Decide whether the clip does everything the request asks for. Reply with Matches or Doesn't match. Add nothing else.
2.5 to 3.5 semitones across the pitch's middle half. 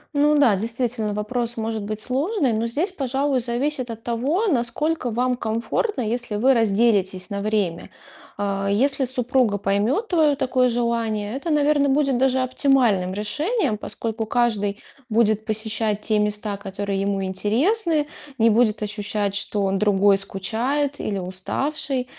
Doesn't match